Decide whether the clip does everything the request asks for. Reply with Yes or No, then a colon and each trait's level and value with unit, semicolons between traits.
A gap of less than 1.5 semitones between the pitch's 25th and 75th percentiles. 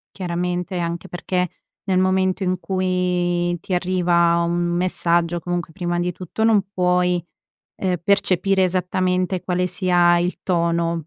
Yes: narrow, 1.1 semitones